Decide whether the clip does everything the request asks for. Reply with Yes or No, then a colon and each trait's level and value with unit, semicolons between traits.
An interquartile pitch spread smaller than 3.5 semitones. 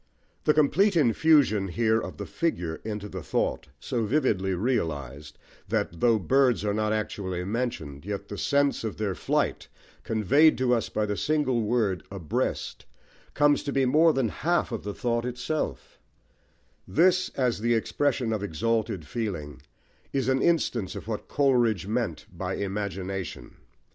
No: average, 5.3 semitones